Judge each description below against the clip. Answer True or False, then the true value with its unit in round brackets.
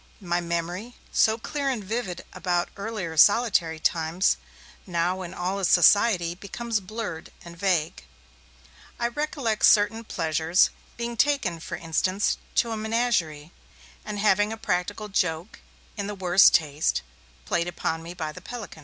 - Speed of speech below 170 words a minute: True (145 wpm)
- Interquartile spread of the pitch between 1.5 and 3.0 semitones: False (4.5 semitones)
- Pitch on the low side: False (190 Hz)